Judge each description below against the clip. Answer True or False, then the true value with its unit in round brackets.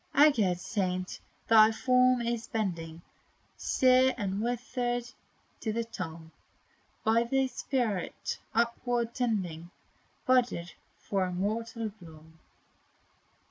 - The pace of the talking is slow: True (95 wpm)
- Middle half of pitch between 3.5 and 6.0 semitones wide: True (4.9 semitones)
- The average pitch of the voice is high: True (225 Hz)